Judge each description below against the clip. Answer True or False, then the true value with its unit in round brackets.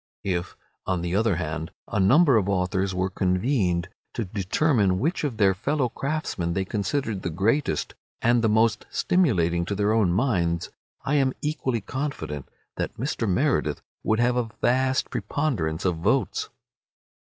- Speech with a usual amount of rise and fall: False (6.3 semitones)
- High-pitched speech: False (105 Hz)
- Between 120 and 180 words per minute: True (155 wpm)